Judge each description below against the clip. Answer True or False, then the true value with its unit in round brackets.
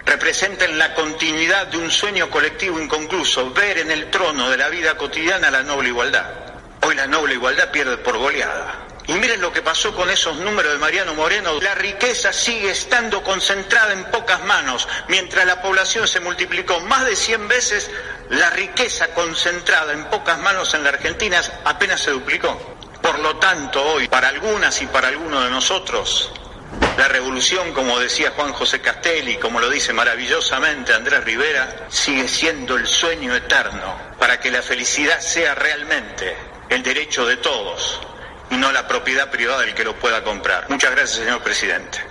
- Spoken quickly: False (170 wpm)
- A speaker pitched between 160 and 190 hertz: True (185 Hz)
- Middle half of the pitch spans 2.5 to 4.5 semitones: False (5.3 semitones)